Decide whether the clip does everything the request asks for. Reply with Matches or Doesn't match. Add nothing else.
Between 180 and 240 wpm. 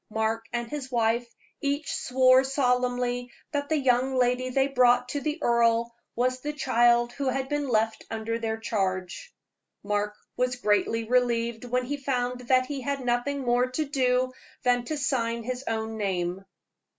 Doesn't match